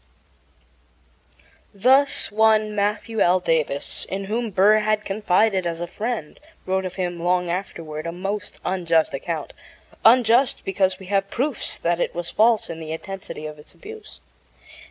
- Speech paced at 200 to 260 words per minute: No, average, 150 wpm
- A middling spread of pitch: Yes, average, 3.8 semitones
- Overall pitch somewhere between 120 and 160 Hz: No, high, 195 Hz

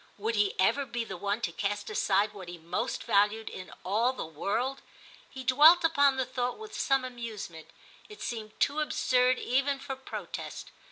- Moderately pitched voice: No, high, 235 Hz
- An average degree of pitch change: Yes, average, 4.7 semitones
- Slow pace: No, average, 180 wpm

